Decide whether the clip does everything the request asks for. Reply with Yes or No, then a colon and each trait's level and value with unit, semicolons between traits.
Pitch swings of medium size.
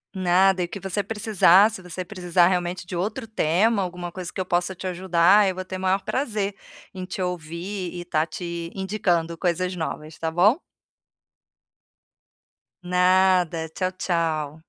No: narrow, 1.8 semitones